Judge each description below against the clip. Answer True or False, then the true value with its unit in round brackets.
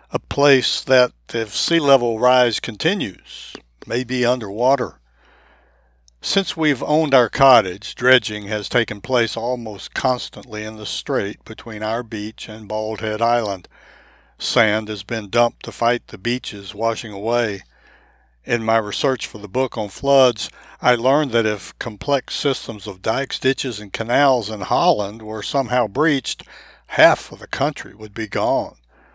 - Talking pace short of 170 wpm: True (150 wpm)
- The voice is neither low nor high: False (115 Hz)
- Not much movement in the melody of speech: False (3.1 semitones)